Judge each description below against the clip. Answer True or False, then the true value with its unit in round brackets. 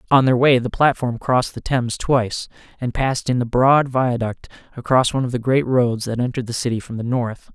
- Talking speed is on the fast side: True (225 wpm)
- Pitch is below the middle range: True (125 Hz)